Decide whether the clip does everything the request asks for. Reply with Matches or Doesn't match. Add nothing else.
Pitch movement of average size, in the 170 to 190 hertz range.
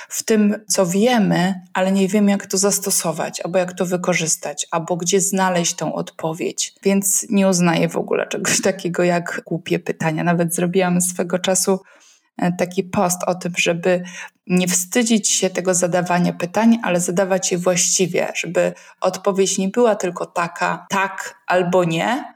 Doesn't match